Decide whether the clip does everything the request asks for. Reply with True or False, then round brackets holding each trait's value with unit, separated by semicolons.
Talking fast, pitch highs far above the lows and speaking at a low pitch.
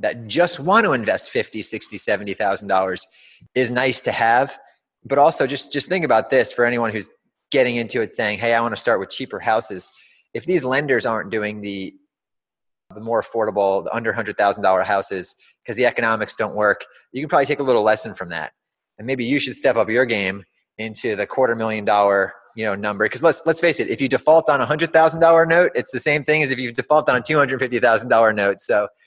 True (230 wpm; 6.3 semitones; 120 Hz)